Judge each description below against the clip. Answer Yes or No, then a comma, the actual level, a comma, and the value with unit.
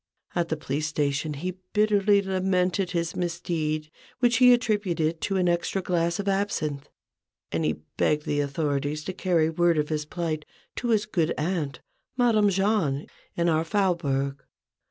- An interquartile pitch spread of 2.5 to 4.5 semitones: Yes, average, 4.1 semitones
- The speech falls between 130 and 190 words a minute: Yes, average, 155 wpm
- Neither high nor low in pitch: Yes, medium, 170 Hz